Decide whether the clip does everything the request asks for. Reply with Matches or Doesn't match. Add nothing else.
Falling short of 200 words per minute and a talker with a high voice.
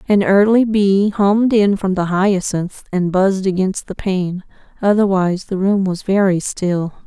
Matches